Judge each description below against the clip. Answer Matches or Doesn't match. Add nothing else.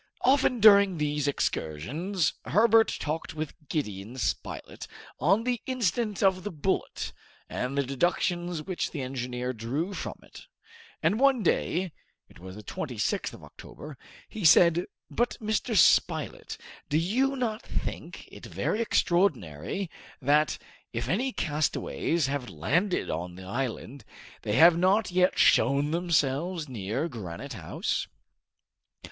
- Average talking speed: Doesn't match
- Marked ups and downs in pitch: Matches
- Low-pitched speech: Doesn't match